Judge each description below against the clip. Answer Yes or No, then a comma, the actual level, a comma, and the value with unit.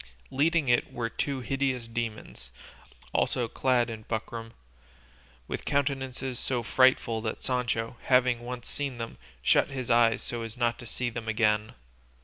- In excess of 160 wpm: No, average, 145 wpm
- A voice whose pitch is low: Yes, low, 120 Hz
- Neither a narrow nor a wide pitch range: No, narrow, 2.1 semitones